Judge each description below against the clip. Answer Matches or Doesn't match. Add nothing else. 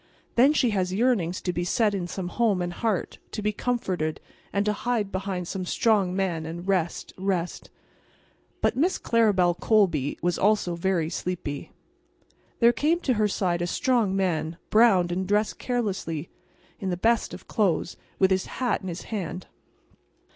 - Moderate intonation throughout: Matches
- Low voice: Doesn't match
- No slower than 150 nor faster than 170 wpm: Matches